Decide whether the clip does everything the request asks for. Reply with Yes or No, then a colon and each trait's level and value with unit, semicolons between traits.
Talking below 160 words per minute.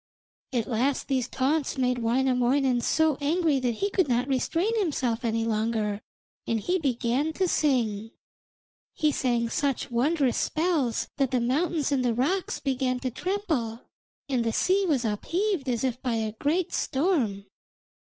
Yes: average, 150 wpm